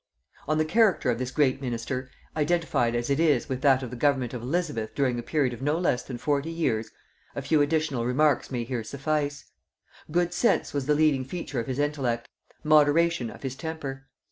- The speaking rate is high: No, average, 195 wpm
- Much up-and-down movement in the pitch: No, average, 3.6 semitones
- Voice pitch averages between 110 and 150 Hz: Yes, medium, 140 Hz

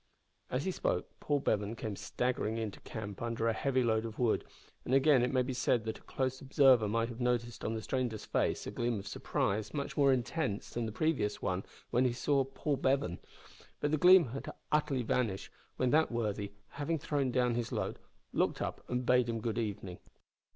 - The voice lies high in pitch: No, low, 120 Hz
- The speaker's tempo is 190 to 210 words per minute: Yes, average, 200 wpm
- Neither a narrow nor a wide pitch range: Yes, average, 3.4 semitones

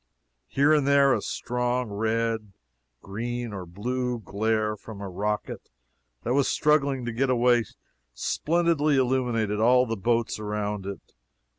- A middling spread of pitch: Yes, average, 3.4 semitones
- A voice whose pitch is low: Yes, low, 120 Hz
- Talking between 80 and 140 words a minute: Yes, slow, 135 wpm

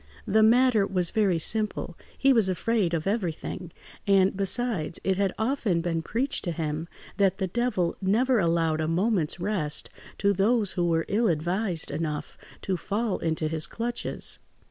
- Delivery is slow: No, average, 160 wpm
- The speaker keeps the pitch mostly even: No, average, 4.7 semitones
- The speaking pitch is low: No, high, 190 Hz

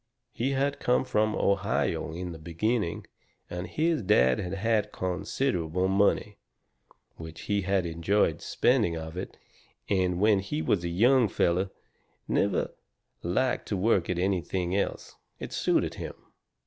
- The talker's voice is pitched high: No, very low, 95 Hz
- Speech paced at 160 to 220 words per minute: No, average, 140 wpm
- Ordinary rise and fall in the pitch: Yes, average, 3.8 semitones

